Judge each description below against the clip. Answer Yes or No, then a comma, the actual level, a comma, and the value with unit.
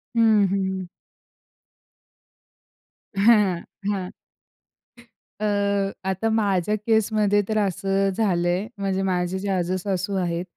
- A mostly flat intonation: Yes, narrow, 1.9 semitones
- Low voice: No, high, 195 Hz